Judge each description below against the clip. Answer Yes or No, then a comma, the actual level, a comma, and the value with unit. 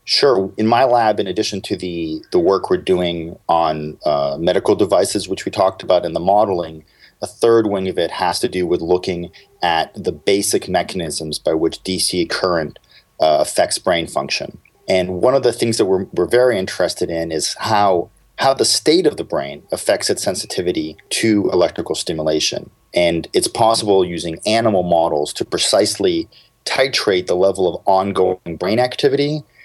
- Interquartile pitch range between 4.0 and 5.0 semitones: No, average, 3.5 semitones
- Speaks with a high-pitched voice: No, very low, 90 Hz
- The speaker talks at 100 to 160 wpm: No, average, 170 wpm